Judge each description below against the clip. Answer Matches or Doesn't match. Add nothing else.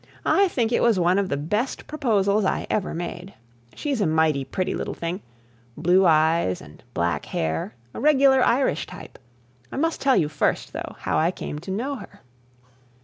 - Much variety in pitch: Matches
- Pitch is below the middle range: Doesn't match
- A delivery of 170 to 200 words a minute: Matches